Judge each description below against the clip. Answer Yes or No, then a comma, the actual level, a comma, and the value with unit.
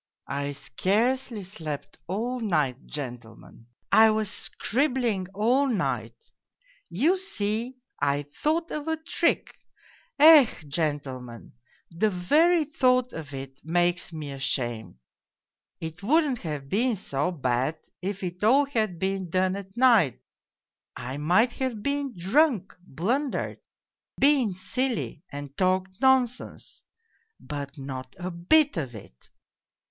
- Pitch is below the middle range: No, high, 190 Hz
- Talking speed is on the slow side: Yes, slow, 120 wpm